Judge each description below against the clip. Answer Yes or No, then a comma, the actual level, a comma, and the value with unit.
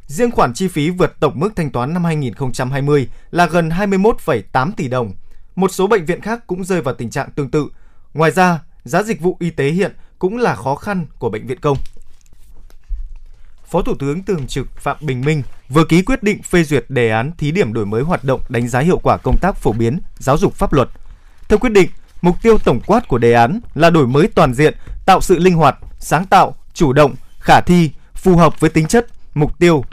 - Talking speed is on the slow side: No, average, 220 wpm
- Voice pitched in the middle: Yes, medium, 155 Hz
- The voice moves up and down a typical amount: No, wide, 6.2 semitones